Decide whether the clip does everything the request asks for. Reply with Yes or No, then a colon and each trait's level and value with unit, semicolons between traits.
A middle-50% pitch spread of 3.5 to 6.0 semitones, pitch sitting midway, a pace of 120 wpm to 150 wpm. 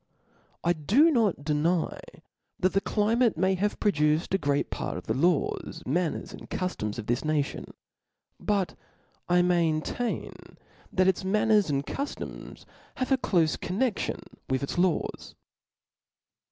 Yes: average, 5.3 semitones; medium, 180 Hz; average, 140 wpm